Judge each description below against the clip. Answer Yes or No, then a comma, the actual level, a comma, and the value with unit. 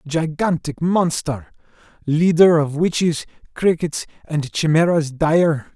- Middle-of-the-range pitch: Yes, medium, 160 Hz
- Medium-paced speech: No, slow, 95 wpm